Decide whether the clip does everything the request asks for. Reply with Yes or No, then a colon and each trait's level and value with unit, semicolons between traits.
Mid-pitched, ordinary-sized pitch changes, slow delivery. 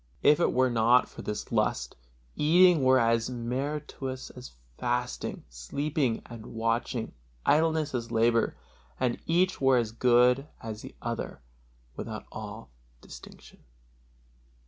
No: low, 125 Hz; average, 3.4 semitones; slow, 125 wpm